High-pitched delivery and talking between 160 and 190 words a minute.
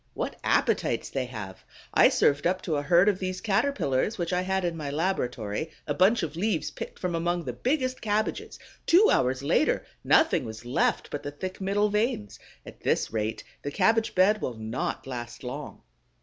No: medium, 170 Hz; average, 185 wpm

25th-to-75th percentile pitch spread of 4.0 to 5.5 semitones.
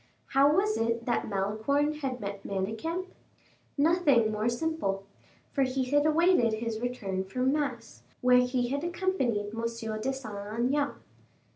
Yes: average, 4.9 semitones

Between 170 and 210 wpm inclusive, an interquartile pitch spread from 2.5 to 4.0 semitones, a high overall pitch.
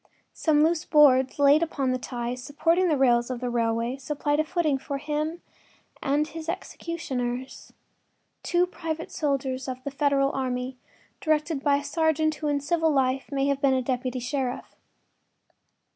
No: average, 155 wpm; average, 3.3 semitones; very high, 280 Hz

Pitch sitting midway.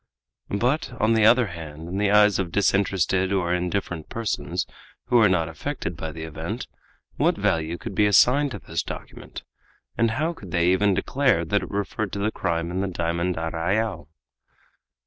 No: very low, 95 Hz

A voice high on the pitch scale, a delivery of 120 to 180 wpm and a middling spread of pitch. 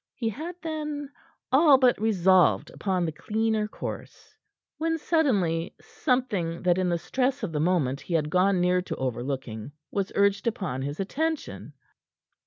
No: high, 195 Hz; average, 150 wpm; wide, 7.7 semitones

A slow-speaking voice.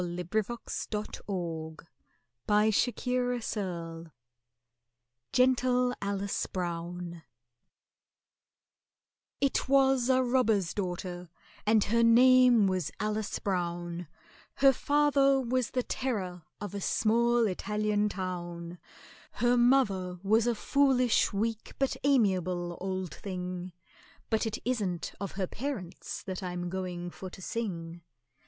Yes: slow, 115 wpm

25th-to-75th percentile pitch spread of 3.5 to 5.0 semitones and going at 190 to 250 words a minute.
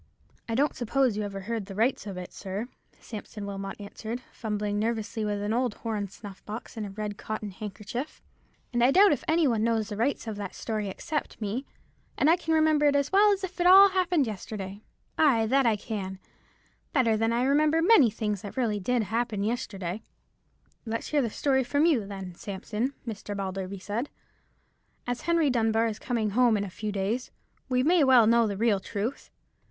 Yes: average, 4.4 semitones; average, 195 wpm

